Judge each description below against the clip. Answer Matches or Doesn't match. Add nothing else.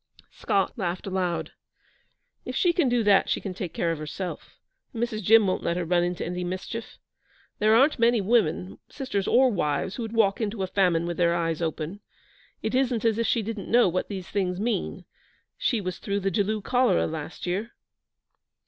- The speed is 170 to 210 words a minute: Matches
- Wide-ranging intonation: Doesn't match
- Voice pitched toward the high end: Matches